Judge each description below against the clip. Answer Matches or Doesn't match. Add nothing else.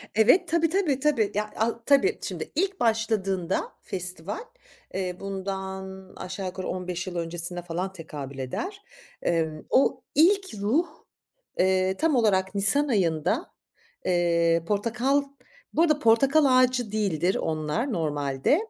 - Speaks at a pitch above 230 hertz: Doesn't match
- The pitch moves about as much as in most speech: Doesn't match